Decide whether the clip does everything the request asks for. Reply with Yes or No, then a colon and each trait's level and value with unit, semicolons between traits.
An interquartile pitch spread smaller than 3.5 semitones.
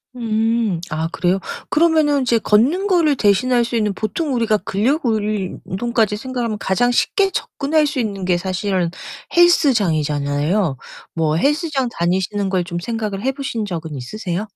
No: wide, 5.5 semitones